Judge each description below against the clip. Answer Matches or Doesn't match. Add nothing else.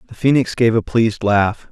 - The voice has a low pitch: Matches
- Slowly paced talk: Doesn't match